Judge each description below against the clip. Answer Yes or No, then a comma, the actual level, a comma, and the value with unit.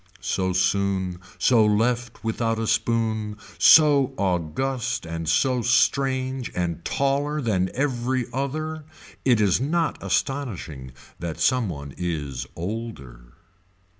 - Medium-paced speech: No, slow, 110 wpm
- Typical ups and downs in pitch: No, wide, 6.7 semitones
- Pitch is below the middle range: Yes, low, 115 Hz